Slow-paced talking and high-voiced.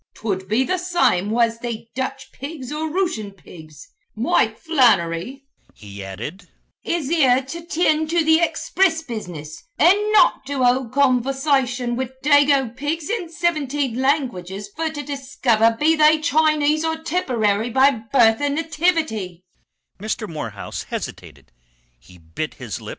Yes: slow, 120 wpm; very high, 265 Hz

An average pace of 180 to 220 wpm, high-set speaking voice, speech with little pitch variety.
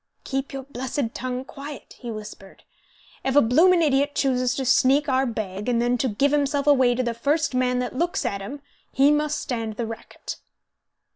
No: average, 190 wpm; very high, 260 Hz; average, 3.1 semitones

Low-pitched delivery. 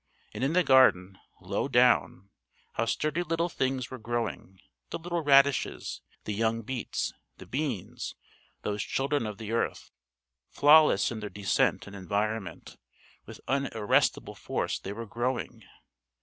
Yes: low, 120 Hz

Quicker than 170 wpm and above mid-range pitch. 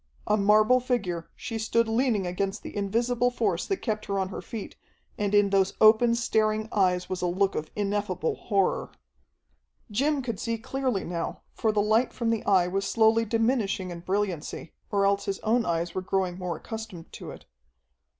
Yes: average, 180 wpm; high, 205 Hz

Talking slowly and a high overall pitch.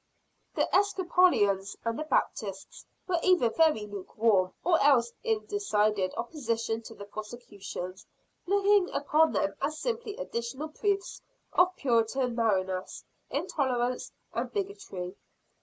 Yes: slow, 115 wpm; high, 245 Hz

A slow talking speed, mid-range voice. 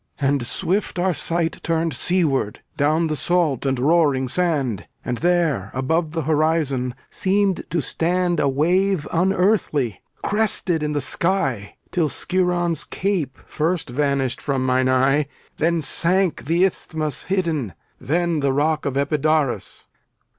Yes: slow, 130 wpm; medium, 155 Hz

